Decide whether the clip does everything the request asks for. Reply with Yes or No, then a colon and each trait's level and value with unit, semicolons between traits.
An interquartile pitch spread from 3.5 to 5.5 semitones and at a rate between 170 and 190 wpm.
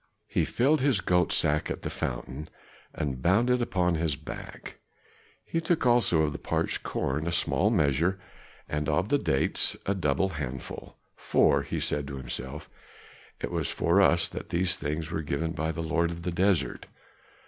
Yes: average, 4.1 semitones; average, 175 wpm